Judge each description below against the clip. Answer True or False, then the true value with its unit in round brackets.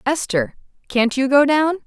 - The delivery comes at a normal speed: True (160 wpm)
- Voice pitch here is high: True (270 Hz)